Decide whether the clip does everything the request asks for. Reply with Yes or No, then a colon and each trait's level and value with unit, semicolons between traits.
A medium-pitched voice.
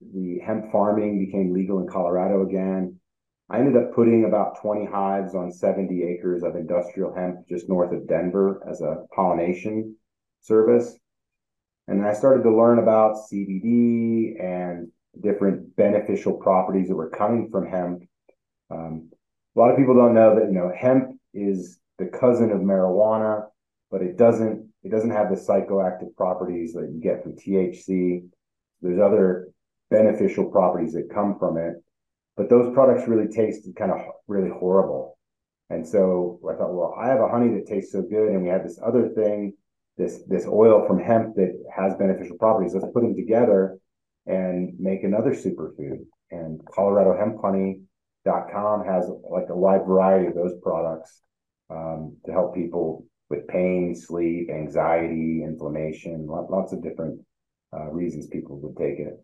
No: very low, 95 Hz